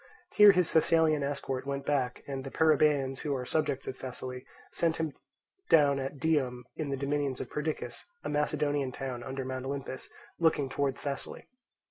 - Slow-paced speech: No, average, 165 wpm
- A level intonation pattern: Yes, narrow, 2.3 semitones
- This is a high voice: No, medium, 140 Hz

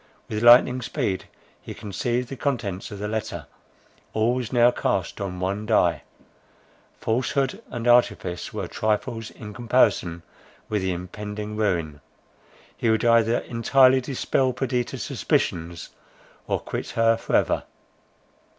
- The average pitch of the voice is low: Yes, low, 110 Hz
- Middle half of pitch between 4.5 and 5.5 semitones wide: No, average, 3.5 semitones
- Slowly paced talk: Yes, slow, 130 wpm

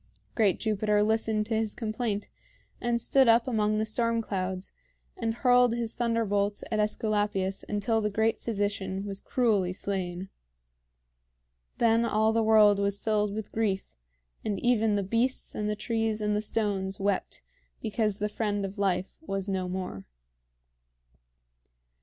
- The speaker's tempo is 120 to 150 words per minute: Yes, average, 145 wpm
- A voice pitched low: No, high, 210 Hz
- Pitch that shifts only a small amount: Yes, narrow, 2.0 semitones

